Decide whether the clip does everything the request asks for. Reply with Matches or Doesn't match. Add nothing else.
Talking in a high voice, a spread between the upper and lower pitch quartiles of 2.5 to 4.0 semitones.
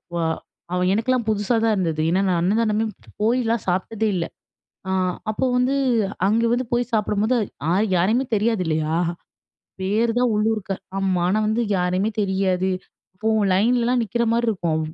Matches